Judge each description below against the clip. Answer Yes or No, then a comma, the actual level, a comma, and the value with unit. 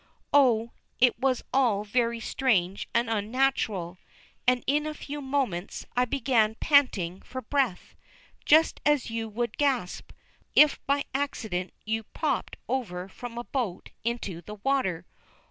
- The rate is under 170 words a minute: Yes, slow, 135 wpm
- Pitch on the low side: No, high, 235 Hz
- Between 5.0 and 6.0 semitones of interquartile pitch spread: No, average, 4.6 semitones